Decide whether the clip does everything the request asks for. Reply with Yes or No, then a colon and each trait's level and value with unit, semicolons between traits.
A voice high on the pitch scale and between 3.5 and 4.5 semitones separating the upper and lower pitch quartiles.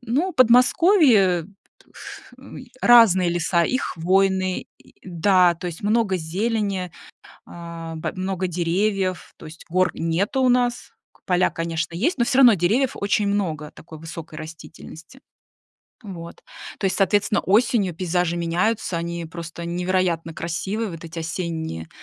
No: medium, 180 Hz; average, 3.8 semitones